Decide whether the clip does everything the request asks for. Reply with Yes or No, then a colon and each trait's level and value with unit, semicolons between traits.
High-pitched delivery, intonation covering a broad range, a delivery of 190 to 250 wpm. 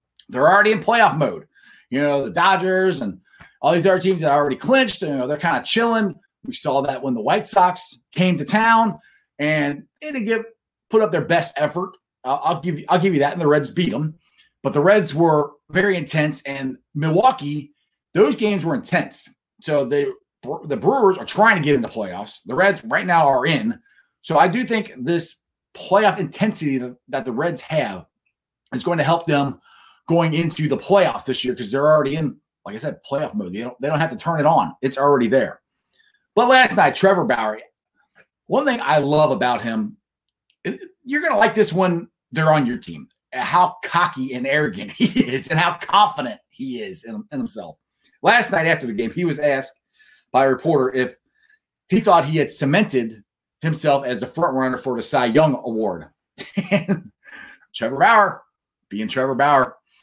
No: medium, 170 Hz; wide, 6.3 semitones; average, 195 wpm